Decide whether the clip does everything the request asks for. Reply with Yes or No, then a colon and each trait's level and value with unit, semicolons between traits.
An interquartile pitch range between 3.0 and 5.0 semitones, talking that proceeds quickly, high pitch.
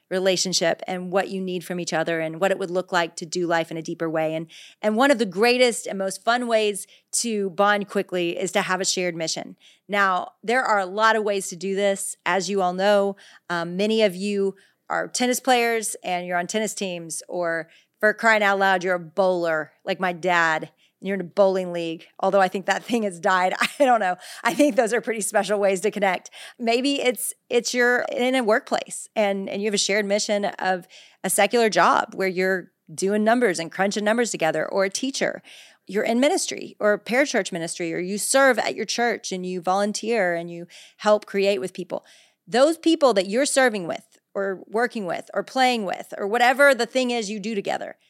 Yes: average, 3.5 semitones; fast, 215 wpm; high, 200 Hz